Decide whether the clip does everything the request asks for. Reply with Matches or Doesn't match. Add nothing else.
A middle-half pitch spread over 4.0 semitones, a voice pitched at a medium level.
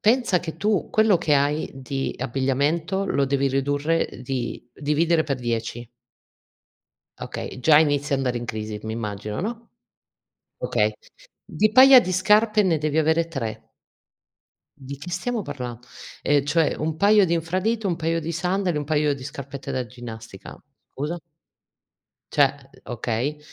Matches